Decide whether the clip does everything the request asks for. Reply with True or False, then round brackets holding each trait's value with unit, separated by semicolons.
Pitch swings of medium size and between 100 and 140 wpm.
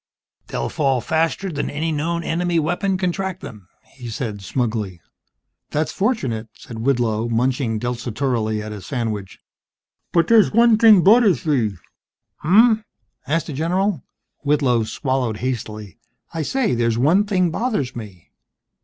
False (7.6 semitones; 135 wpm)